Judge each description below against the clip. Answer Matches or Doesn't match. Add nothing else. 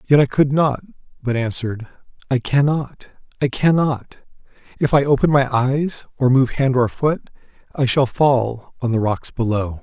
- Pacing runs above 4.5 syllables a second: Doesn't match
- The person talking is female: Doesn't match